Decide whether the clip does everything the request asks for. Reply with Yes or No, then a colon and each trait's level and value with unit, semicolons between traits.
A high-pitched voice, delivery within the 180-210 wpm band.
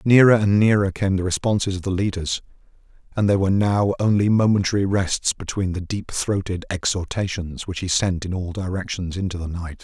No: very low, 95 Hz; average, 185 wpm